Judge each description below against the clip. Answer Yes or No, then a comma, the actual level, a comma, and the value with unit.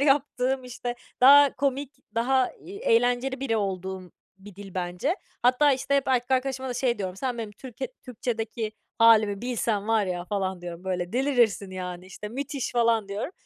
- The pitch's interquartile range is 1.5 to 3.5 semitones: No, average, 4.8 semitones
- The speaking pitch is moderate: No, high, 235 Hz